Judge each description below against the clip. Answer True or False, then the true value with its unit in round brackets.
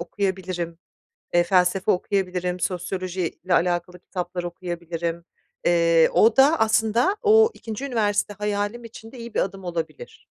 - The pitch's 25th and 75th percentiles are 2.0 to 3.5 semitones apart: False (3.9 semitones)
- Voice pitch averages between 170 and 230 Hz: True (185 Hz)